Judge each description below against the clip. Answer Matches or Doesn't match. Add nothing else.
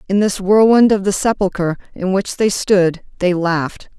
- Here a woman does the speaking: Matches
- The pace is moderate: Matches